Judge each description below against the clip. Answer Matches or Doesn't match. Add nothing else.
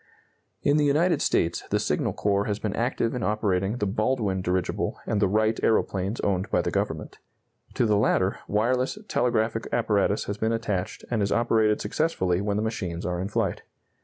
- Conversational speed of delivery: Matches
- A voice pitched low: Matches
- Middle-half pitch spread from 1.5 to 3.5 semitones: Matches